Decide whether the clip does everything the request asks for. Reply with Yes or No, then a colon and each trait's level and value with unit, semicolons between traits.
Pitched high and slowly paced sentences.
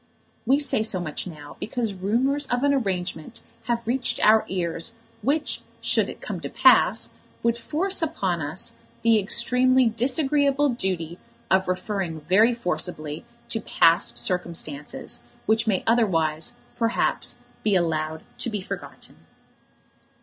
Yes: high, 215 Hz; slow, 130 wpm